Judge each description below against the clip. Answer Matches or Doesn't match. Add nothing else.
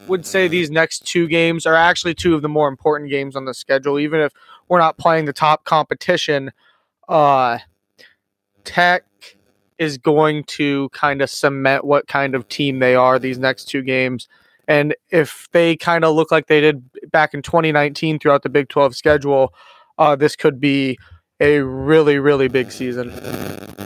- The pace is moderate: Matches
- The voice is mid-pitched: Matches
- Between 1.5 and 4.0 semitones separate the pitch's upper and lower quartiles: Matches